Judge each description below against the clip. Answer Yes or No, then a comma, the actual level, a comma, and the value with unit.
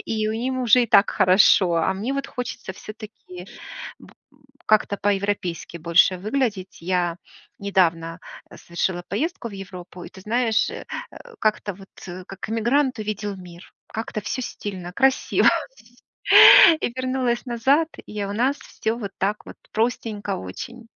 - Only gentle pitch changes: No, average, 4.3 semitones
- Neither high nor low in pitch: No, high, 205 Hz